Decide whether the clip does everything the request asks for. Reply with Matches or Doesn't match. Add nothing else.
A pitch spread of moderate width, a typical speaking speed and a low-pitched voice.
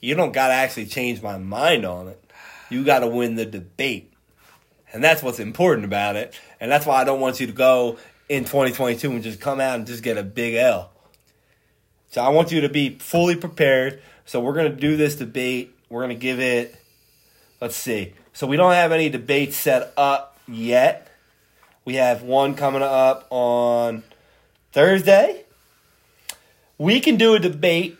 Matches